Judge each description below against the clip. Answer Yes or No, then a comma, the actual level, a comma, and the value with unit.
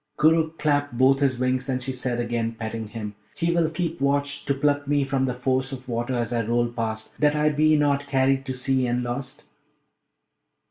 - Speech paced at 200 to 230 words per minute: Yes, fast, 205 wpm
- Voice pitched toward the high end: No, low, 130 Hz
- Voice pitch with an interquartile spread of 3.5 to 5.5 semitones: No, average, 3.0 semitones